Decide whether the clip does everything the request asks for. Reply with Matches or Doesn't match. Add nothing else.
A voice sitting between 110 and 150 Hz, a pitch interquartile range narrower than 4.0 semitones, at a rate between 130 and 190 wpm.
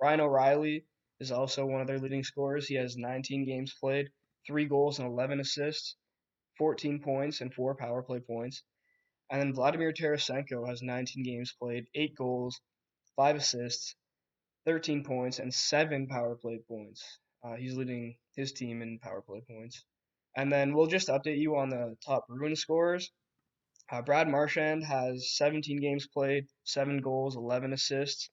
Matches